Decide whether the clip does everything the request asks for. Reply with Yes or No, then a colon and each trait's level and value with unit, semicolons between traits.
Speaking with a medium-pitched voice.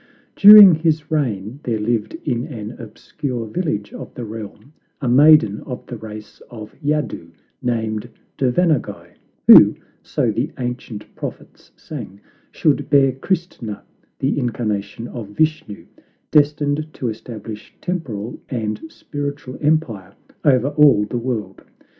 No: low, 125 Hz